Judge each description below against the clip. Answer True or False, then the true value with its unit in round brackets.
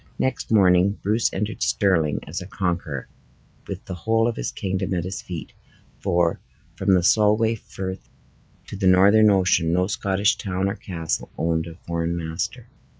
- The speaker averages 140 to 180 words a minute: True (160 wpm)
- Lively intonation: False (3.1 semitones)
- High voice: False (95 Hz)